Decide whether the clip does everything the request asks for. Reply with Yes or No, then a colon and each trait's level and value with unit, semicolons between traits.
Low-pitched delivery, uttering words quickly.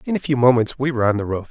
Yes: low, 125 Hz; fast, 360 wpm